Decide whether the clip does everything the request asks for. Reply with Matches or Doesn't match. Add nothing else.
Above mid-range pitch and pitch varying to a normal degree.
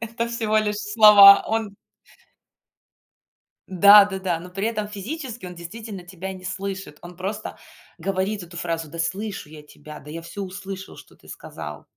Matches